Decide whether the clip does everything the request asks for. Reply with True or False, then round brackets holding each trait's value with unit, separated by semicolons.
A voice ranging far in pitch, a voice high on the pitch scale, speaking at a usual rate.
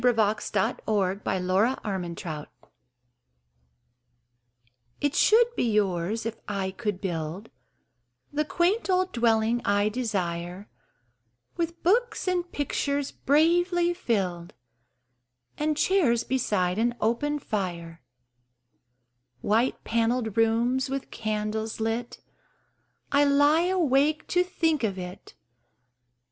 False (6.7 semitones; 230 Hz; 100 wpm)